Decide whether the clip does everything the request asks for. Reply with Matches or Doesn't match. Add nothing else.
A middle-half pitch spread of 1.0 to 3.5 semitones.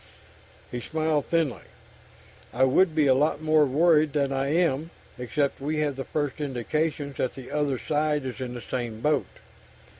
Matches